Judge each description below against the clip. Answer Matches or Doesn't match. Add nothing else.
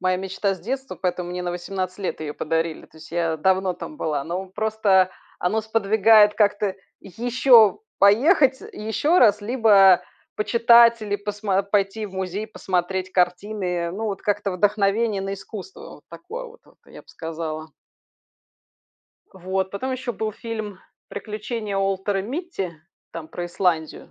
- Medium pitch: Doesn't match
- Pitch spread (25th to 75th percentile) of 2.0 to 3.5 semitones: Matches